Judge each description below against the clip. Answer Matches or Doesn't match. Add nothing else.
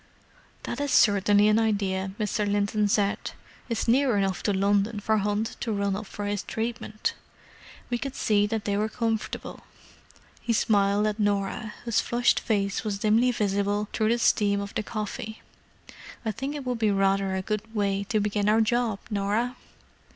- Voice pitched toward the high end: Matches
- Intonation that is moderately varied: Doesn't match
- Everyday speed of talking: Matches